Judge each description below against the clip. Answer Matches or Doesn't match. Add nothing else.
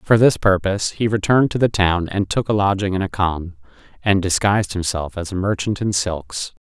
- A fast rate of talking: Matches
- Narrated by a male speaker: Matches